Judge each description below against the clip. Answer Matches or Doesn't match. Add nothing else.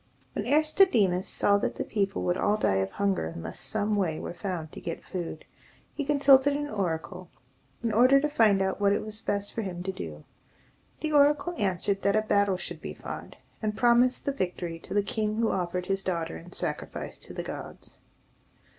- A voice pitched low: Doesn't match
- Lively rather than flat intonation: Doesn't match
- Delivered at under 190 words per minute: Doesn't match